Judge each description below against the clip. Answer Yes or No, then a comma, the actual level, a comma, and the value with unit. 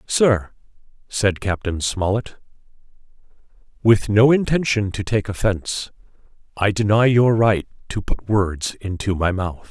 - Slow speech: Yes, slow, 125 wpm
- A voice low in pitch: Yes, low, 105 Hz